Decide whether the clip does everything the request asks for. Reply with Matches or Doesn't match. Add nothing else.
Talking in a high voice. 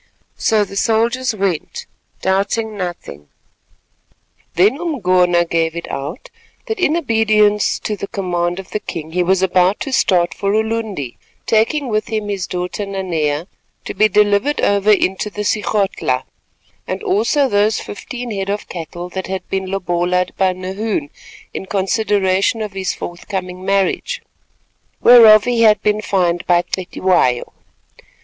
Matches